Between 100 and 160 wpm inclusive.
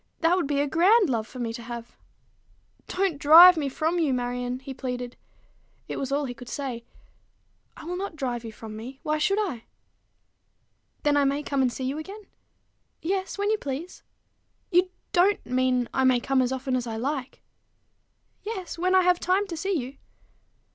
No: average, 190 wpm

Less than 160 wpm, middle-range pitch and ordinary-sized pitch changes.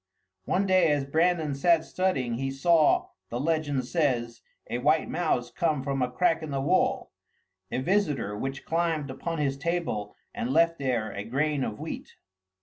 No: average, 165 wpm; medium, 145 Hz; average, 4.2 semitones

